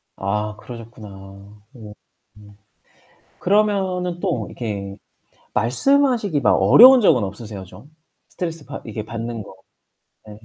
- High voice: No, low, 115 Hz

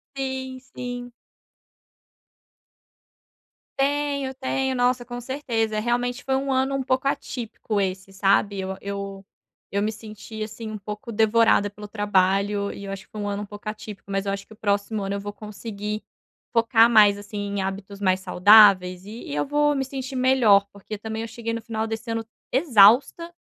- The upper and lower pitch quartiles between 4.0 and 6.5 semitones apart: No, average, 3.6 semitones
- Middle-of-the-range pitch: No, high, 215 Hz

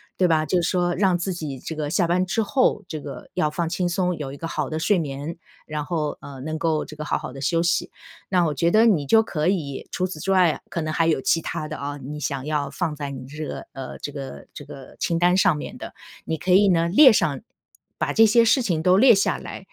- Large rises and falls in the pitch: No, average, 3.5 semitones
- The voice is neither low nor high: Yes, medium, 165 Hz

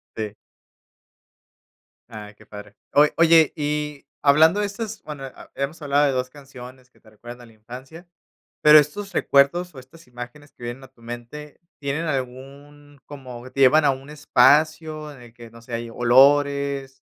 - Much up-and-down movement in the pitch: No, average, 3.4 semitones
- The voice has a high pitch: No, medium, 140 Hz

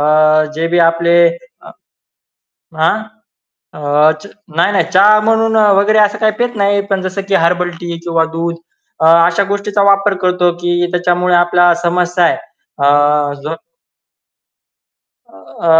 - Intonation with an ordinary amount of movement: Yes, average, 3.3 semitones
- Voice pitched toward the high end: No, medium, 175 Hz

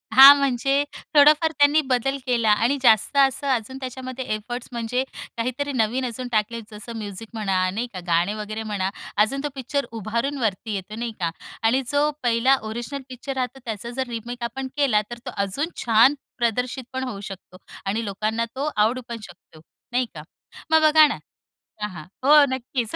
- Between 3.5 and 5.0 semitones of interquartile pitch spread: Yes, average, 3.8 semitones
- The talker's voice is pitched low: No, high, 240 Hz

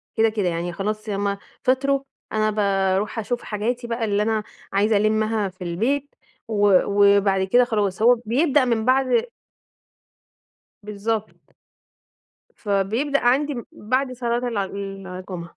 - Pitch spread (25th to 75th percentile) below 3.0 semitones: No, average, 3.5 semitones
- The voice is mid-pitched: No, high, 215 Hz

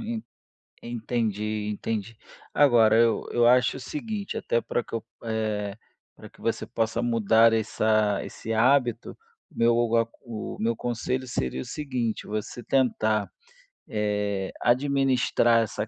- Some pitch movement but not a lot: No, narrow, 2.1 semitones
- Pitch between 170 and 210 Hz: No, low, 115 Hz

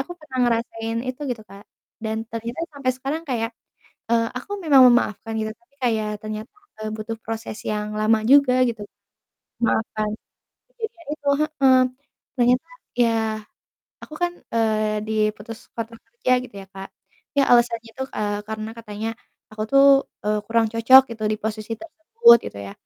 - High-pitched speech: Yes, high, 230 Hz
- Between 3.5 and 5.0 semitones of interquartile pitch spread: No, average, 3.1 semitones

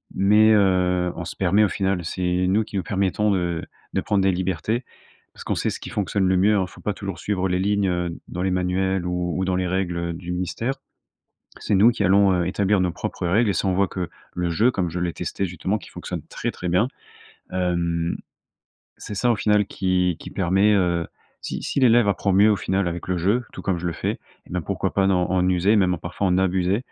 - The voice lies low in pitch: Yes, very low, 95 Hz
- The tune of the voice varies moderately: No, narrow, 2.1 semitones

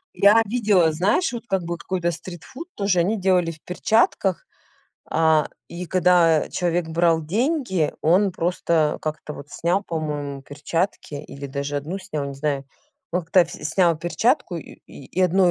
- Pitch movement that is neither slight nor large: Yes, average, 3.6 semitones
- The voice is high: No, medium, 170 Hz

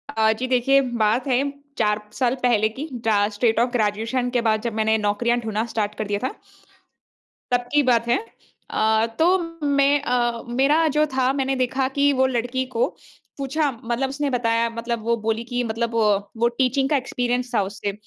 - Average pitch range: Yes, average, 3.0 semitones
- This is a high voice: Yes, high, 240 Hz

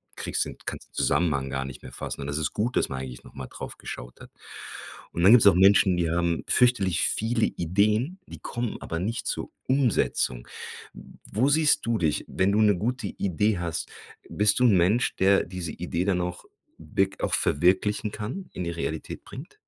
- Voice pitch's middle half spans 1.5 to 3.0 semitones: No, average, 4.7 semitones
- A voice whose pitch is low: Yes, very low, 95 Hz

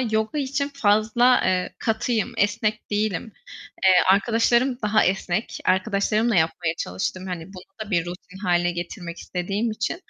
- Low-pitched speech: No, high, 205 Hz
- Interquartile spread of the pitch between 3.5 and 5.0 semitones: Yes, average, 3.8 semitones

